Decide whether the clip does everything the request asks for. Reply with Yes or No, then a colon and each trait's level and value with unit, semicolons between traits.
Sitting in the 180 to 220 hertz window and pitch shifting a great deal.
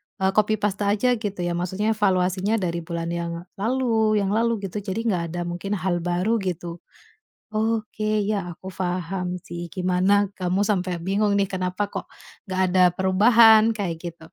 No: high, 190 Hz; average, 3.1 semitones